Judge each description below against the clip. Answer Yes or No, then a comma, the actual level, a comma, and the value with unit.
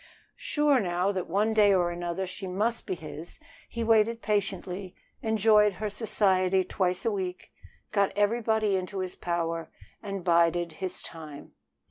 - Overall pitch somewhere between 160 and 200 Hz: Yes, high, 190 Hz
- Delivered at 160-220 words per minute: No, average, 145 wpm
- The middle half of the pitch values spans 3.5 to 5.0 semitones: No, average, 3.1 semitones